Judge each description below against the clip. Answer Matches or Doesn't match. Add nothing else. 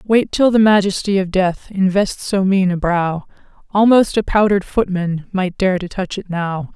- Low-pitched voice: Doesn't match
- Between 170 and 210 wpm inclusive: Matches